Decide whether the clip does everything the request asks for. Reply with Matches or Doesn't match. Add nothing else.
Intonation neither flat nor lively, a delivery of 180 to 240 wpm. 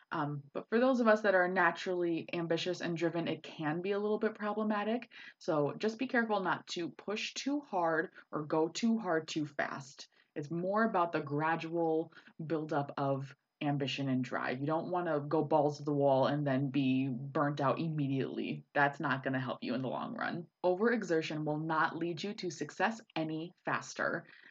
Matches